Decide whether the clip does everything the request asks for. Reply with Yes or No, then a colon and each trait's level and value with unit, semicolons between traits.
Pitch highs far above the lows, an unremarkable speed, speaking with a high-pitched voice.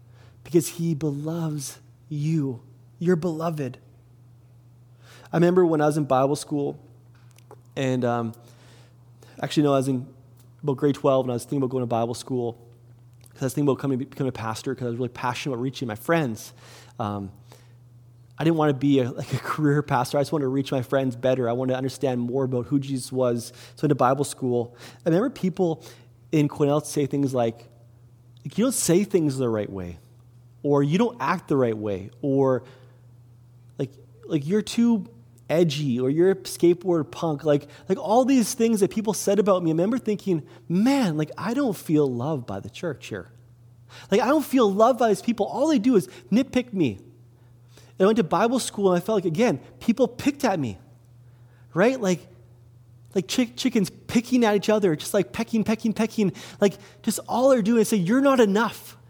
No: wide, 6.8 semitones; average, 195 wpm; low, 135 Hz